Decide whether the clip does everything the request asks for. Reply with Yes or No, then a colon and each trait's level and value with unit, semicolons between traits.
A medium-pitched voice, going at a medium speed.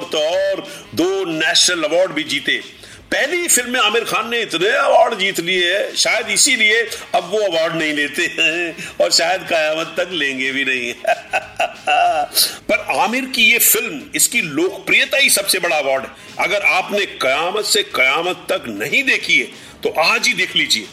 No: very high, 275 Hz; average, 150 wpm